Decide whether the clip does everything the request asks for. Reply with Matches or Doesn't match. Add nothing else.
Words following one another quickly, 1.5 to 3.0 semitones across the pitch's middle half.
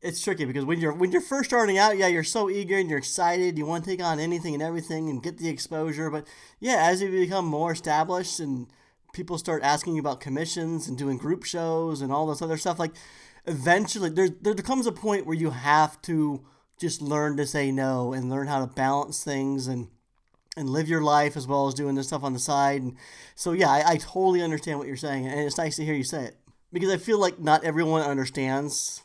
Doesn't match